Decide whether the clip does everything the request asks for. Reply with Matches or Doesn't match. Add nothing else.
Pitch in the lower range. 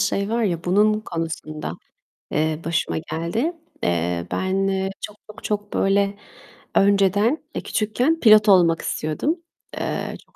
Doesn't match